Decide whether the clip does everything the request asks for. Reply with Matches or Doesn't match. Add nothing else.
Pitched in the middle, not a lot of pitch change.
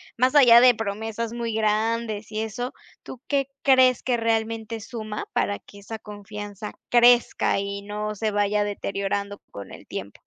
Doesn't match